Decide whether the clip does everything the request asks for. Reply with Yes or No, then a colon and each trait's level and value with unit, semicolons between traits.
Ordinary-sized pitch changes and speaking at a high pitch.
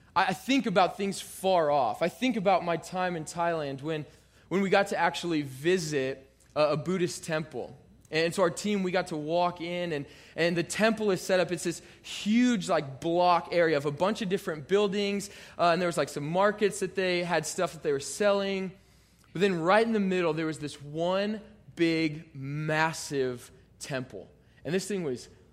No: average, 3.9 semitones; medium, 170 Hz